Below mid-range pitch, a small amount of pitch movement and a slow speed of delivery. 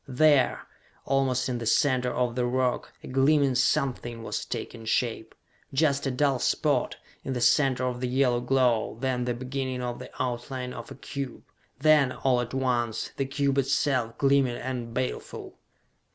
No: low, 130 Hz; narrow, 1.9 semitones; average, 165 wpm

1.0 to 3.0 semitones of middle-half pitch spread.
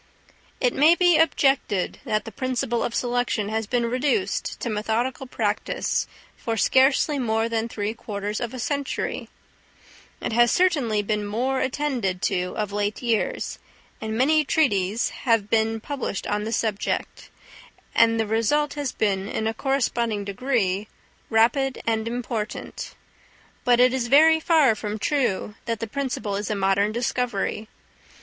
No: average, 3.8 semitones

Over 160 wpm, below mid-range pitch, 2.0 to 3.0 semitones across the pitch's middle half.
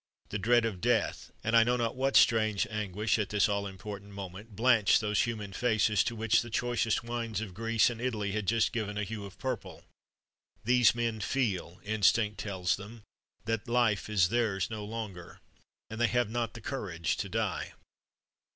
Yes: average, 180 wpm; low, 110 Hz; narrow, 2.4 semitones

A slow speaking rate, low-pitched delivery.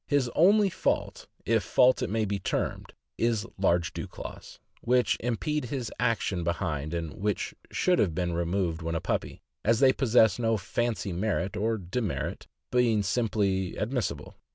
No: average, 160 wpm; low, 110 Hz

